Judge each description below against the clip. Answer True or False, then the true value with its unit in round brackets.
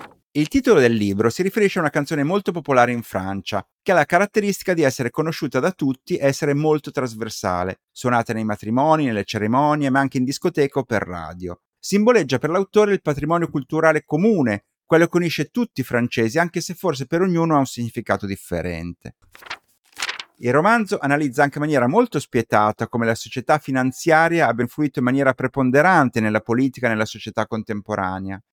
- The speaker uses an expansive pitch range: True (6.0 semitones)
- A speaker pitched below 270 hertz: True (135 Hz)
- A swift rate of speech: True (175 wpm)